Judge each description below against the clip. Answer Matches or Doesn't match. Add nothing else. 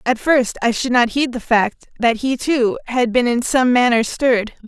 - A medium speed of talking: Doesn't match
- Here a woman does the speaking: Matches